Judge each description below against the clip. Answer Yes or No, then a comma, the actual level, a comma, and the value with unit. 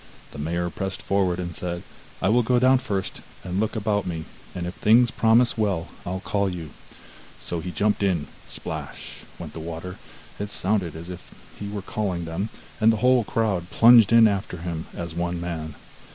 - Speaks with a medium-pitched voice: No, very low, 95 Hz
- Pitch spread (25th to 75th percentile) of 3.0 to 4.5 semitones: Yes, average, 3.9 semitones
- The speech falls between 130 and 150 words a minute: No, average, 185 wpm